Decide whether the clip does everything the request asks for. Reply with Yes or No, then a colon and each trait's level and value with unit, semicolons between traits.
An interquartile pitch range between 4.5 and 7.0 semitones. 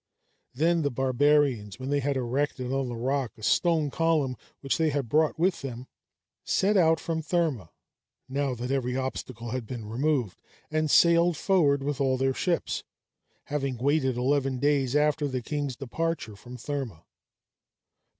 No: average, 3.2 semitones